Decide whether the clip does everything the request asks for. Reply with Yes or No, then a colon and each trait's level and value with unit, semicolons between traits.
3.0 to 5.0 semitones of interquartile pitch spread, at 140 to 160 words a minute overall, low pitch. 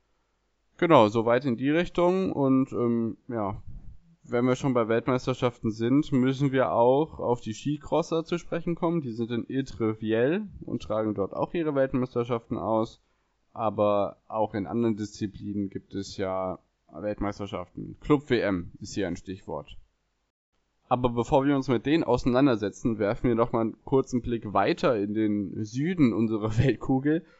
Yes: average, 4.1 semitones; average, 155 wpm; low, 120 Hz